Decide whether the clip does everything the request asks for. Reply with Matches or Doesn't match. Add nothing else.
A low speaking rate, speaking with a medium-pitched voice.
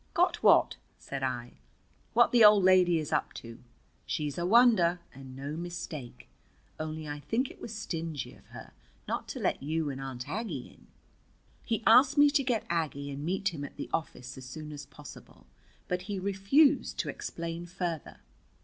Doesn't match